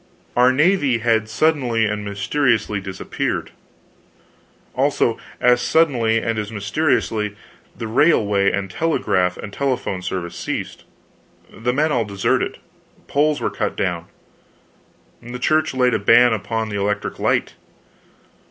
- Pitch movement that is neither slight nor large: Yes, average, 4.1 semitones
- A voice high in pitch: No, low, 115 Hz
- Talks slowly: Yes, slow, 125 wpm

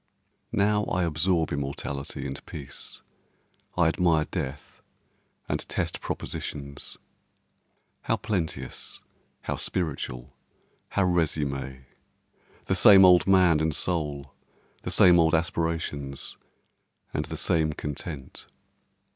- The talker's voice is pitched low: Yes, very low, 80 Hz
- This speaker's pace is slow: Yes, slow, 95 wpm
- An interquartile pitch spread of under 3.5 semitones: No, average, 3.9 semitones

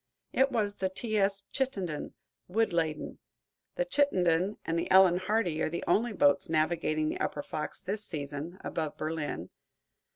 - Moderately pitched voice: Yes, medium, 180 Hz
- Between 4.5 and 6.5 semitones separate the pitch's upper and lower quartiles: Yes, average, 5.0 semitones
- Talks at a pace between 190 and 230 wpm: No, average, 155 wpm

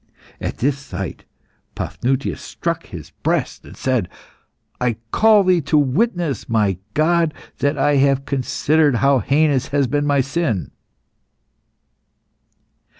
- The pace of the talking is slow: Yes, slow, 120 wpm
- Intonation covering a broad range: No, average, 3.1 semitones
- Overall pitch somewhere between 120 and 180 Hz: Yes, medium, 140 Hz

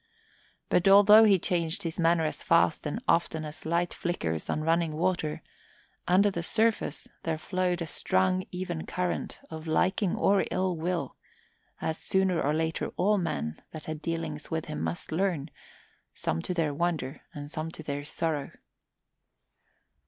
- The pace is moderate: Yes, average, 155 wpm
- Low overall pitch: No, medium, 165 Hz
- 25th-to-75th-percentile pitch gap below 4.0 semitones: Yes, average, 2.7 semitones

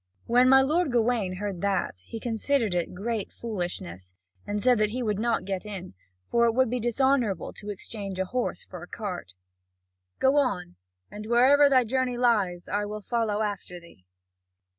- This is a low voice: No, high, 215 Hz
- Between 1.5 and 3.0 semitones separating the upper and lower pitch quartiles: No, average, 4.5 semitones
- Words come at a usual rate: Yes, average, 175 wpm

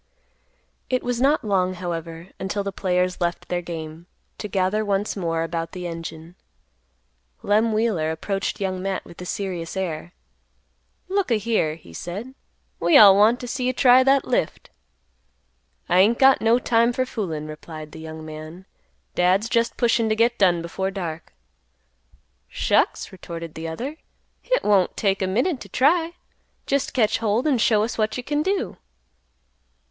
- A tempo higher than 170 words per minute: No, average, 165 wpm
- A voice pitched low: No, high, 195 Hz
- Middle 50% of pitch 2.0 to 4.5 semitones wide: No, wide, 5.6 semitones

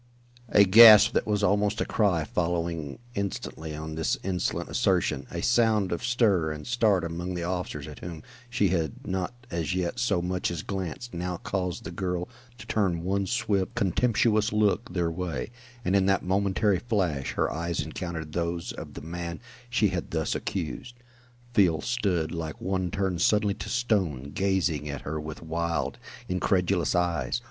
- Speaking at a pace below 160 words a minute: No, average, 165 wpm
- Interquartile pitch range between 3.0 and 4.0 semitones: Yes, average, 3.3 semitones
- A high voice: No, very low, 90 Hz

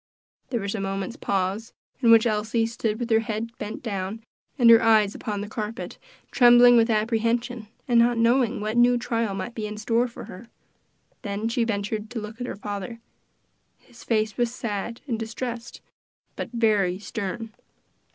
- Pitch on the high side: Yes, high, 225 Hz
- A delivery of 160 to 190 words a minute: Yes, average, 170 wpm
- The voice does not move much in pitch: Yes, narrow, 2.1 semitones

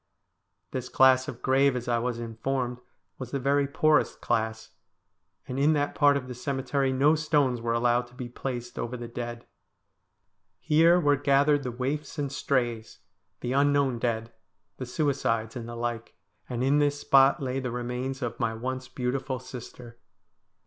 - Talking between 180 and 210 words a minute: No, average, 165 wpm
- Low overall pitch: Yes, low, 130 Hz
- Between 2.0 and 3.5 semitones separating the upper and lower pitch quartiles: Yes, average, 2.7 semitones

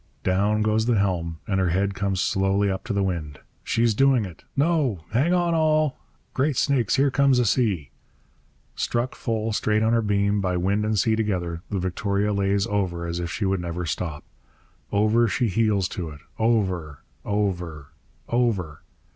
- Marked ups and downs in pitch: No, average, 4.0 semitones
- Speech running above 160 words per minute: Yes, average, 170 wpm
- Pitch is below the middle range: Yes, low, 100 Hz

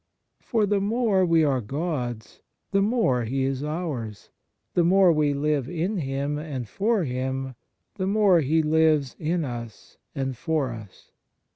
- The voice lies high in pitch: No, medium, 150 Hz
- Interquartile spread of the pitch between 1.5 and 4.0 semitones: No, average, 5.3 semitones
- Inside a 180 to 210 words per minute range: No, average, 155 wpm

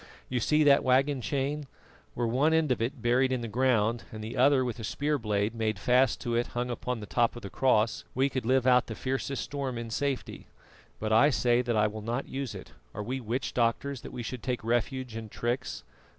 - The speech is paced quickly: Yes, fast, 225 wpm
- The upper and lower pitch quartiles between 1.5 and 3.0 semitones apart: Yes, average, 2.7 semitones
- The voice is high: No, low, 125 Hz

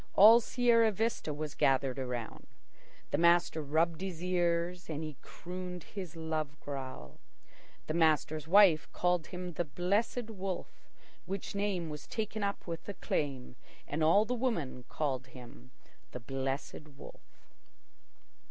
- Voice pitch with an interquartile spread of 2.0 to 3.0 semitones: No, average, 4.8 semitones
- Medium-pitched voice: Yes, medium, 165 Hz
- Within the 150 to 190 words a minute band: No, slow, 135 wpm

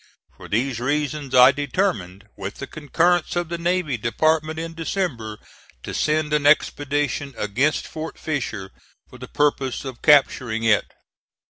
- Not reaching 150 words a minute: Yes, average, 140 wpm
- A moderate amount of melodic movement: Yes, average, 4.2 semitones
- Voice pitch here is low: No, medium, 145 Hz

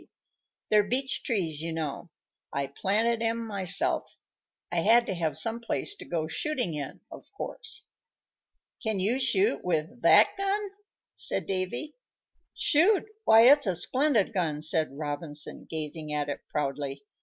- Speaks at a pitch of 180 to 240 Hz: Yes, high, 190 Hz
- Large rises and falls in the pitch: Yes, wide, 7.3 semitones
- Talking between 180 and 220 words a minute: No, average, 145 wpm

